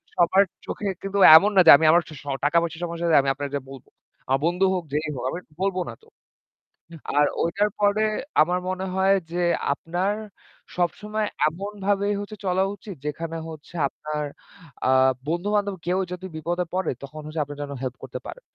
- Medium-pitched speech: Yes, medium, 175 Hz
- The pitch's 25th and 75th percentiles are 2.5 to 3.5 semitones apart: No, average, 4.2 semitones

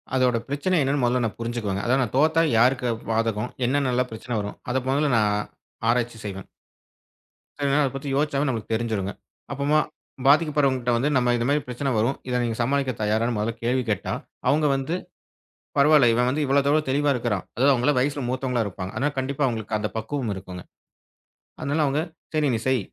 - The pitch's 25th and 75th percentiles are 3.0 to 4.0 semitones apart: Yes, average, 3.6 semitones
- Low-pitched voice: Yes, low, 125 Hz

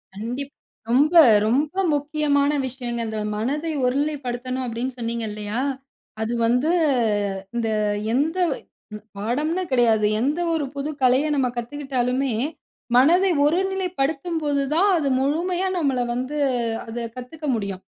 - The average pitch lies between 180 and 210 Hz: No, very high, 270 Hz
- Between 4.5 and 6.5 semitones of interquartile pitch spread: No, average, 3.9 semitones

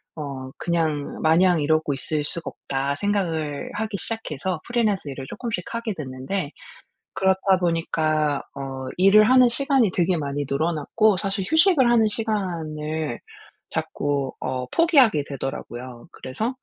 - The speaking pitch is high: No, medium, 165 Hz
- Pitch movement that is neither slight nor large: No, wide, 6.8 semitones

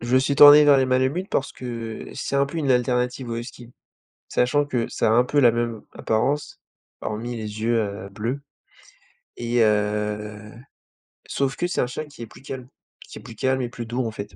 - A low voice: Yes, low, 120 Hz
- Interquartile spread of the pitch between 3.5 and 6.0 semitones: No, average, 3.1 semitones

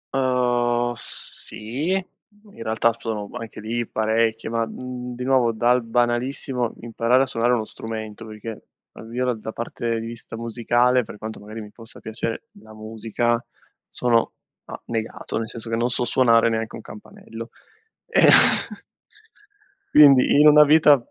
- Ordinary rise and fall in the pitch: No, narrow, 1.9 semitones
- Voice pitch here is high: No, low, 115 Hz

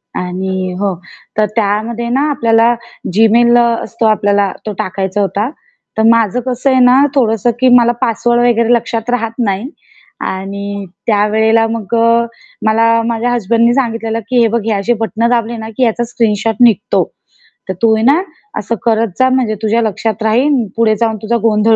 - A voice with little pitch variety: Yes, narrow, 1.8 semitones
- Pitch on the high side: Yes, high, 225 Hz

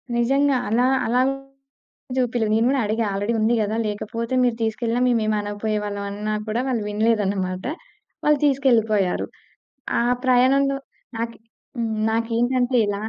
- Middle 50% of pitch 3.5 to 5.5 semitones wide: No, average, 2.8 semitones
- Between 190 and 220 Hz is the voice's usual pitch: No, high, 230 Hz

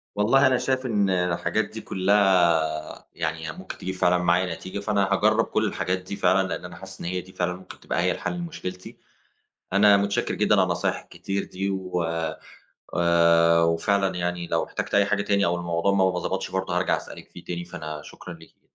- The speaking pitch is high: No, very low, 95 Hz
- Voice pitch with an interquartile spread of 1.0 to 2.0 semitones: No, narrow, 2.5 semitones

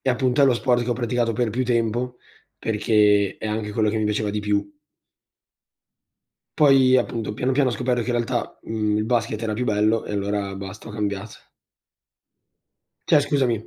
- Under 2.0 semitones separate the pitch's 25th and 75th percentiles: No, average, 2.9 semitones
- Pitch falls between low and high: No, low, 115 Hz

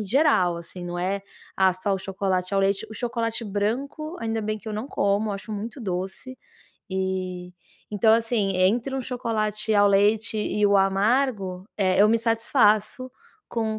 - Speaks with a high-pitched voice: Yes, high, 210 Hz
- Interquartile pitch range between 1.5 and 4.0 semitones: Yes, average, 2.9 semitones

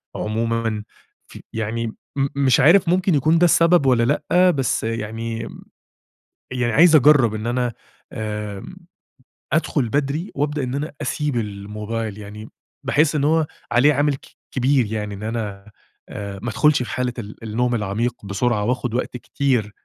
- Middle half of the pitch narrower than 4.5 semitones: No, average, 5.0 semitones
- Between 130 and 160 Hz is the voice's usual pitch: No, low, 120 Hz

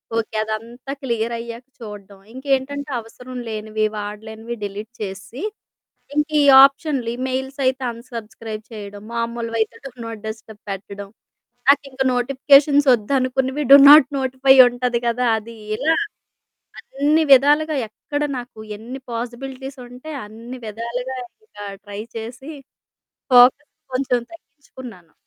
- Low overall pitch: No, high, 245 Hz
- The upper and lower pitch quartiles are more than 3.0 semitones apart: Yes, average, 3.5 semitones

